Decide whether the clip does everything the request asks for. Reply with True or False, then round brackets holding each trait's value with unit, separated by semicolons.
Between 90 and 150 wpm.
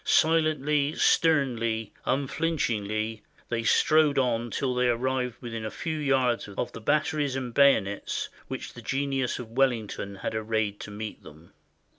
True (140 wpm)